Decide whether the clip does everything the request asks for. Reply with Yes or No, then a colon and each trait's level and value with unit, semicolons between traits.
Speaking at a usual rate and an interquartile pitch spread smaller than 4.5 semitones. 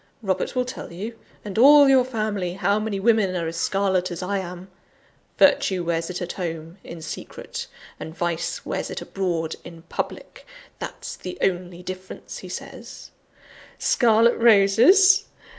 Yes: average, 150 wpm; average, 4.0 semitones